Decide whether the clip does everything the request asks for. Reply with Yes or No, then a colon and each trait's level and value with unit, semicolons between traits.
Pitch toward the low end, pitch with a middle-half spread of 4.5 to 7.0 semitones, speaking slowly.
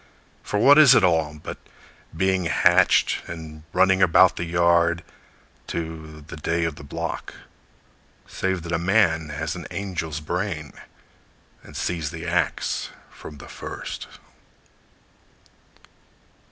No: very low, 85 Hz; average, 2.8 semitones; slow, 125 wpm